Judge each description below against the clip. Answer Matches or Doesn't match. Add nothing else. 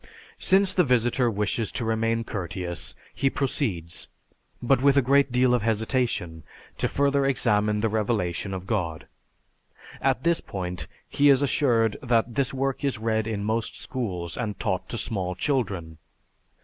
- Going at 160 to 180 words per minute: Doesn't match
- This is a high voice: Doesn't match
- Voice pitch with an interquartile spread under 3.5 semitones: Doesn't match